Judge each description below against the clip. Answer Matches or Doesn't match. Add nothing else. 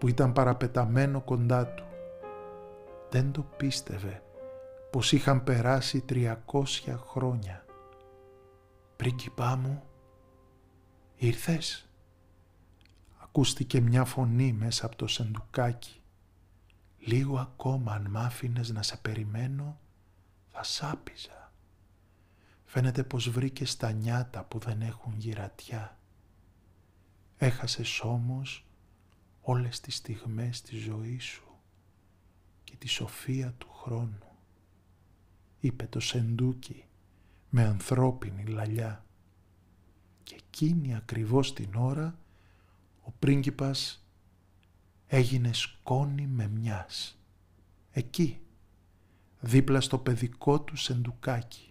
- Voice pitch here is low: Matches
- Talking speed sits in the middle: Doesn't match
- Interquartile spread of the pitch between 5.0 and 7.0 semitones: Matches